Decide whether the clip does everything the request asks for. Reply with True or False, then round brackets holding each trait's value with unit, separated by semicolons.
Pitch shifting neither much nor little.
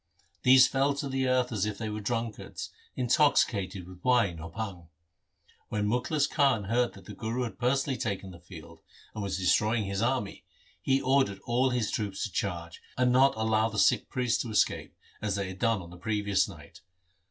True (4.4 semitones)